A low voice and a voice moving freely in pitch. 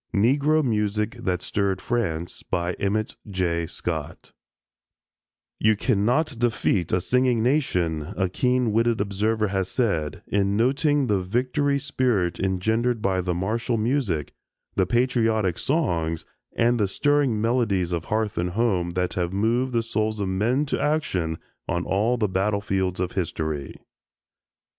No: low, 105 Hz; average, 4.8 semitones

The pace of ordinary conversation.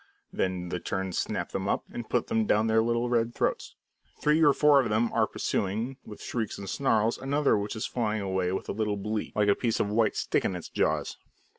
No: fast, 225 wpm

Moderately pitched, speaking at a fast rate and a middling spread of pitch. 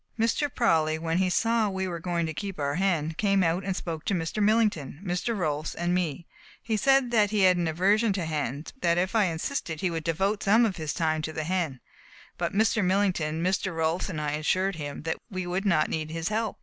Yes: medium, 180 Hz; fast, 220 wpm; average, 3.9 semitones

